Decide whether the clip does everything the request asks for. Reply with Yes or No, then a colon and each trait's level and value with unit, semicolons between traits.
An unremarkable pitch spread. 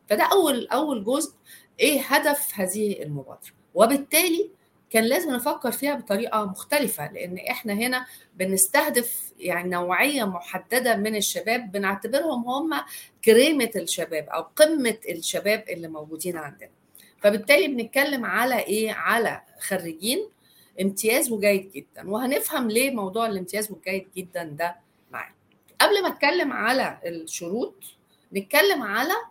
No: wide, 6.6 semitones